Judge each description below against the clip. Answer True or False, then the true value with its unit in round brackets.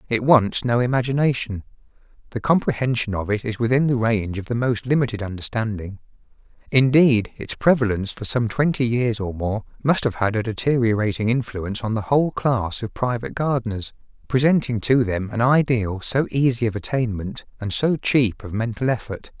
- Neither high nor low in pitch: False (115 Hz)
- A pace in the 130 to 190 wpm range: True (165 wpm)